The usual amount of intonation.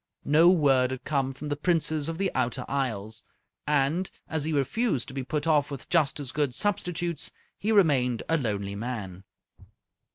Yes: average, 4.2 semitones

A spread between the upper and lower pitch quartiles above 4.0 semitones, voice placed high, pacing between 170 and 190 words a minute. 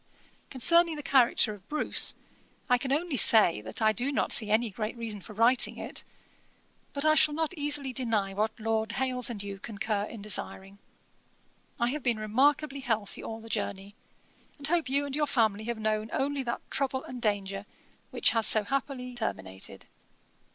Yes: average, 4.4 semitones; high, 235 Hz; average, 175 wpm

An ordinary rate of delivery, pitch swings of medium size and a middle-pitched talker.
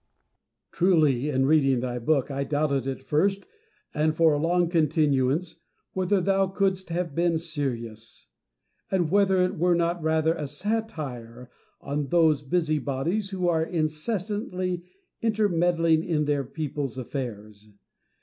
No: slow, 130 wpm; average, 4.4 semitones; medium, 160 Hz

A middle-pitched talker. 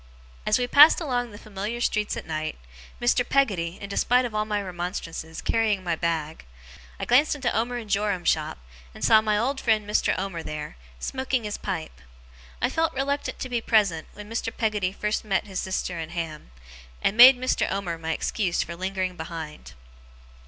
No: high, 205 Hz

